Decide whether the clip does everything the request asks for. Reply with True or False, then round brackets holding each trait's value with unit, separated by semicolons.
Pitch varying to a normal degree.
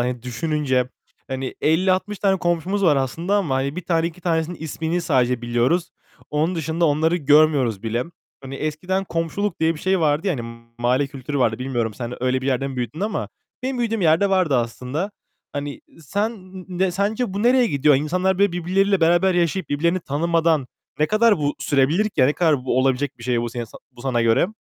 False (5.7 semitones)